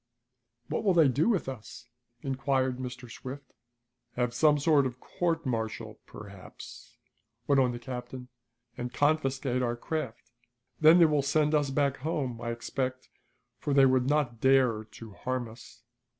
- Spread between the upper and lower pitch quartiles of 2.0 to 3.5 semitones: Yes, average, 2.9 semitones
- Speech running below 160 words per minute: Yes, average, 150 wpm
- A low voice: Yes, low, 130 Hz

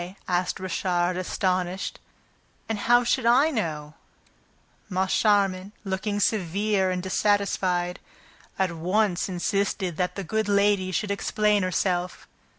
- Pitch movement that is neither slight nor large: No, narrow, 2.3 semitones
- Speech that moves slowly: Yes, slow, 110 wpm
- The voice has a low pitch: No, high, 190 Hz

